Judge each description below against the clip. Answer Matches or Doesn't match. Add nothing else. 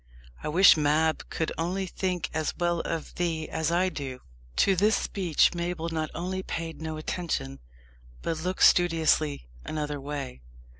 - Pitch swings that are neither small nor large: Doesn't match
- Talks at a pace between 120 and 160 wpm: Matches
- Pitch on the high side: Doesn't match